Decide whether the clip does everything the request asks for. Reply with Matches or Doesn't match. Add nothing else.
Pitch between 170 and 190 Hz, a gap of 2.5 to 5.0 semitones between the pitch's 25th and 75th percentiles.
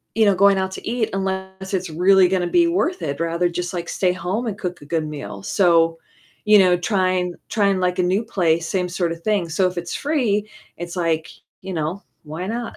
Matches